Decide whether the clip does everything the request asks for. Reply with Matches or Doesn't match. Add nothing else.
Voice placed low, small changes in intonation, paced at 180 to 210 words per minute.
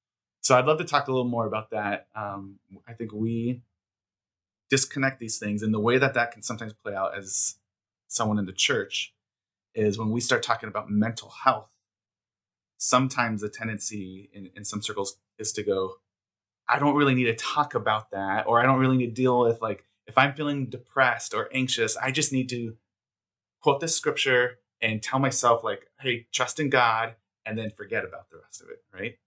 Doesn't match